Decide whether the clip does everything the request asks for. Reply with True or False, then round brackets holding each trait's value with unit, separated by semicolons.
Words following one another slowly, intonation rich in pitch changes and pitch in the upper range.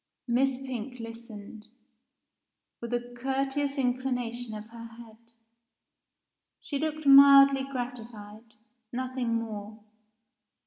False (90 wpm; 2.8 semitones; 245 Hz)